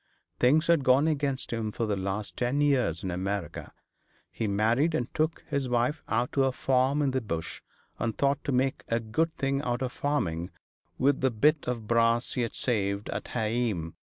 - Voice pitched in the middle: No, low, 125 Hz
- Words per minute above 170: Yes, average, 185 wpm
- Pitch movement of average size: Yes, average, 4.3 semitones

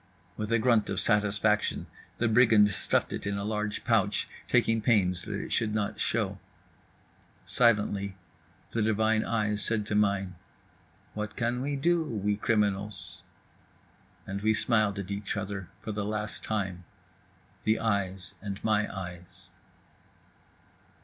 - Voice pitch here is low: Yes, low, 105 Hz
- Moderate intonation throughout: No, narrow, 1.8 semitones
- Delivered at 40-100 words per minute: No, slow, 135 wpm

